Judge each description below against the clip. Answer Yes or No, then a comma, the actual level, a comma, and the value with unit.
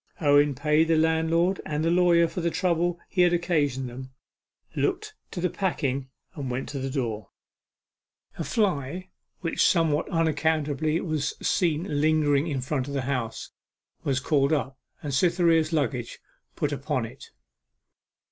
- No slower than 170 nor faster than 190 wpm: No, average, 145 wpm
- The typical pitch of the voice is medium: Yes, medium, 155 Hz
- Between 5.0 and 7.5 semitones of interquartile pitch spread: No, average, 3.5 semitones